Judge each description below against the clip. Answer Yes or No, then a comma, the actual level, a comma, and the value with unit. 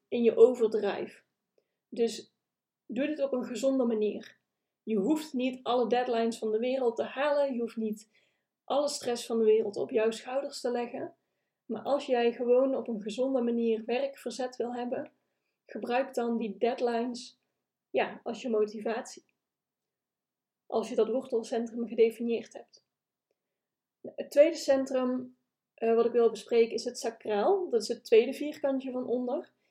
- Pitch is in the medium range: No, high, 240 Hz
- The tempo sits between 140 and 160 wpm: Yes, average, 150 wpm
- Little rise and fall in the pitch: Yes, narrow, 2.3 semitones